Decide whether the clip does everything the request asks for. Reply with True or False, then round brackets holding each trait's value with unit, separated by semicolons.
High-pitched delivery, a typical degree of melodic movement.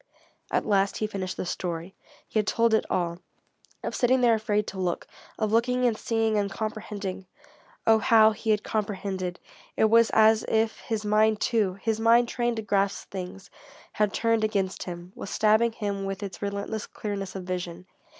False (210 Hz; 2.3 semitones)